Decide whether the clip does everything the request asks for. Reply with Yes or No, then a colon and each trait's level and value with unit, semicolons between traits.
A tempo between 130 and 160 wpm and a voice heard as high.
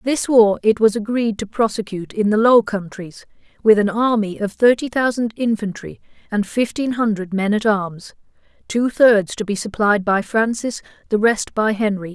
No: average, 175 wpm; high, 215 Hz